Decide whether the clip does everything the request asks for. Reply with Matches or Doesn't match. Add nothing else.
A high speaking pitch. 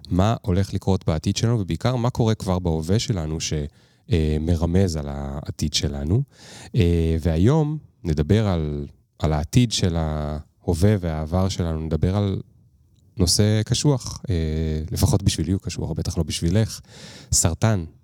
Doesn't match